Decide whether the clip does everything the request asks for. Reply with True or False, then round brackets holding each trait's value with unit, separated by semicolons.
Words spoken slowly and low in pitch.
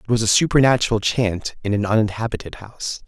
False (175 wpm; 110 Hz)